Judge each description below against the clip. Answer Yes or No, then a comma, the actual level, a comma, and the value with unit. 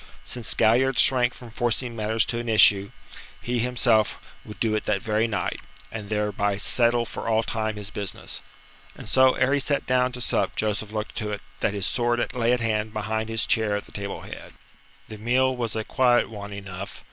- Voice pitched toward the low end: Yes, low, 110 Hz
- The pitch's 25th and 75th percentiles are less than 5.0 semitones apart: Yes, narrow, 2.5 semitones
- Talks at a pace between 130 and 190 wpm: No, average, 200 wpm